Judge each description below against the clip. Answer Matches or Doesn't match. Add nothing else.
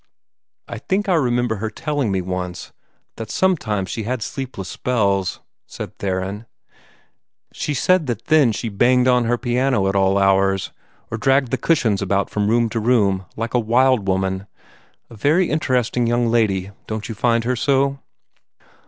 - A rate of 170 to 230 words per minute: Doesn't match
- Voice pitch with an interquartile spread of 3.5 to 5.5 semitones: Matches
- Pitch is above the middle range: Doesn't match